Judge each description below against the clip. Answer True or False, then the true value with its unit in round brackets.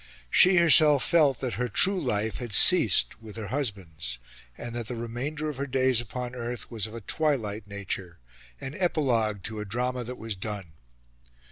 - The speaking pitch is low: True (120 Hz)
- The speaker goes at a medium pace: True (175 wpm)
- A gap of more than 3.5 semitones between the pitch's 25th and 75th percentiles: True (4.4 semitones)